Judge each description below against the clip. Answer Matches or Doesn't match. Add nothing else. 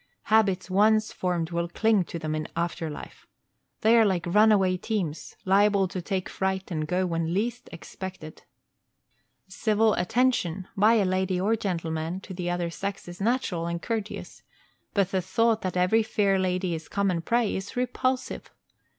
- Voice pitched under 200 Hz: Matches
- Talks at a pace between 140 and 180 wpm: Matches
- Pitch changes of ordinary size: Matches